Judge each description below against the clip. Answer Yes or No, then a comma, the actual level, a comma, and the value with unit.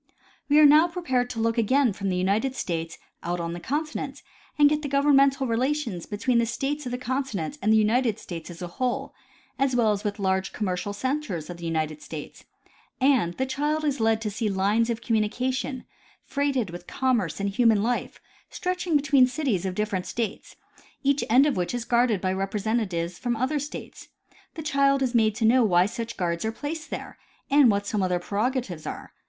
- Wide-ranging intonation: Yes, wide, 5.7 semitones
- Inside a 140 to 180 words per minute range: No, average, 195 wpm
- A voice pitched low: No, high, 230 Hz